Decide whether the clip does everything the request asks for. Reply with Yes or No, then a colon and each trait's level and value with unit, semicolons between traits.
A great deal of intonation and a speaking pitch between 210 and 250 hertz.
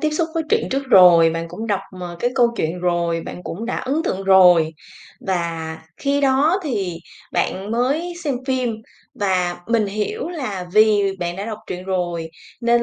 No: wide, 6.5 semitones; high, 200 Hz